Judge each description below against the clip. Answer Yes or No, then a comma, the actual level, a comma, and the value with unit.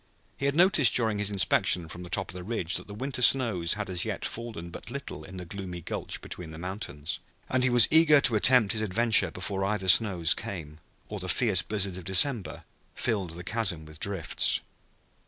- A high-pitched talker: No, low, 100 Hz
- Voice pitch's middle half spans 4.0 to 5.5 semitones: Yes, average, 4.6 semitones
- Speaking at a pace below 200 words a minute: No, fast, 205 wpm